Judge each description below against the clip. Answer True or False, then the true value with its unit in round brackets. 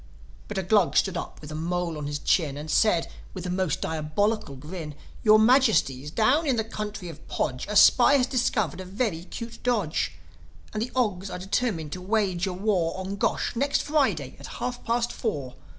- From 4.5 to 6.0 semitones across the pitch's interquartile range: True (5.6 semitones)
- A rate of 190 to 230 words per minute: True (195 wpm)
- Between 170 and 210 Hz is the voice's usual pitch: True (190 Hz)